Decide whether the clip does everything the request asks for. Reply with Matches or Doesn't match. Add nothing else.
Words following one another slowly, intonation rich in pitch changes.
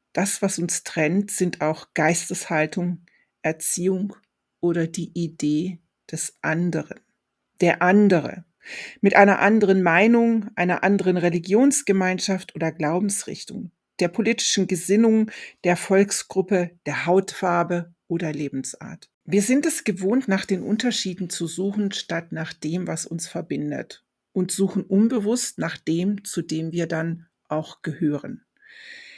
Doesn't match